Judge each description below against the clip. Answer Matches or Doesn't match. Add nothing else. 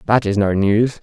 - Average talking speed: Doesn't match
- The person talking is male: Matches